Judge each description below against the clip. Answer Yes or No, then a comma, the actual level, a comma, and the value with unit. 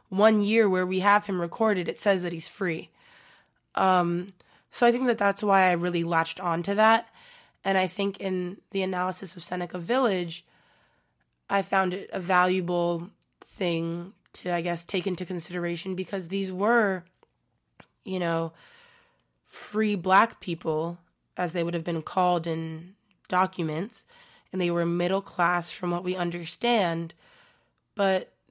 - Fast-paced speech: No, average, 150 wpm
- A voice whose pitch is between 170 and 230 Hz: Yes, medium, 185 Hz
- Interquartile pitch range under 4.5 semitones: Yes, narrow, 2.6 semitones